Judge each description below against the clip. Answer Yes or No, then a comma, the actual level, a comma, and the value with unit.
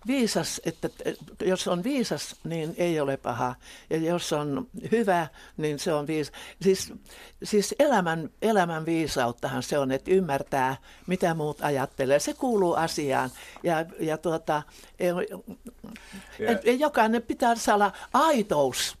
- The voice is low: No, medium, 175 Hz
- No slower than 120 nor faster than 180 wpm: Yes, average, 135 wpm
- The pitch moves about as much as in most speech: No, wide, 6.1 semitones